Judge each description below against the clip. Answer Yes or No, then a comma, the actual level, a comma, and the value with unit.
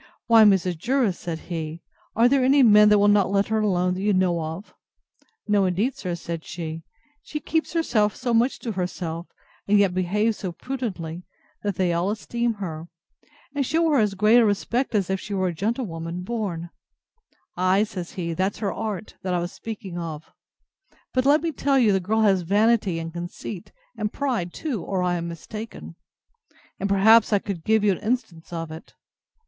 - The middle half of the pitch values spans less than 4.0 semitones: No, average, 4.3 semitones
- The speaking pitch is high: Yes, high, 200 Hz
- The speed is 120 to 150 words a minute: No, average, 190 wpm